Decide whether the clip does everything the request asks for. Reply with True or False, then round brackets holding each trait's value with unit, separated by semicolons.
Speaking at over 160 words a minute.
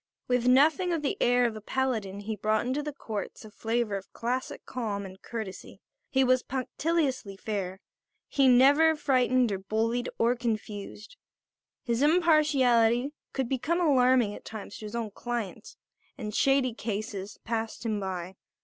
False (155 wpm)